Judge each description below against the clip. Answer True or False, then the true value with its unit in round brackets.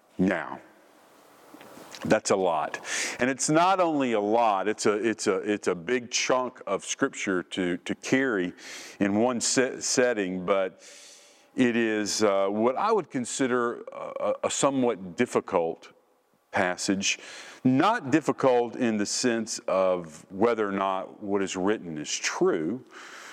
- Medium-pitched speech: False (110 Hz)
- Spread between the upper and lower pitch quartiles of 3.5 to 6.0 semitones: True (4.4 semitones)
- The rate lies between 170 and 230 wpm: False (140 wpm)